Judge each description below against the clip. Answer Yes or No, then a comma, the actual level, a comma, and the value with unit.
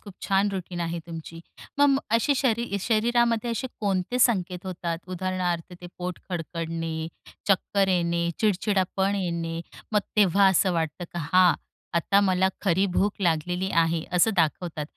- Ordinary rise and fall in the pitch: Yes, average, 3.0 semitones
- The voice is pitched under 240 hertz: Yes, medium, 185 Hz